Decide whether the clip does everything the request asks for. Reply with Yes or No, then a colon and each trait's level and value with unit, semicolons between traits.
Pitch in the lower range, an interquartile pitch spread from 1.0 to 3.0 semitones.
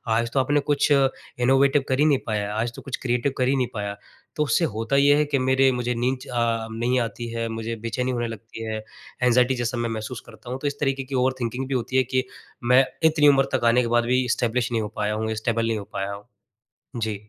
Yes: low, 125 Hz; average, 2.7 semitones